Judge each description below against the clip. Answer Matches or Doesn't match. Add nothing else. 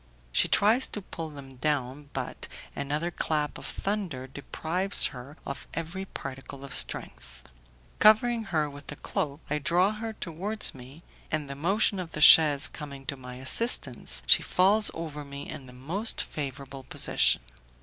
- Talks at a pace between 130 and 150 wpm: Doesn't match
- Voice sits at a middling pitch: Matches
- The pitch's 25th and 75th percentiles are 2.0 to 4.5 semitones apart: Doesn't match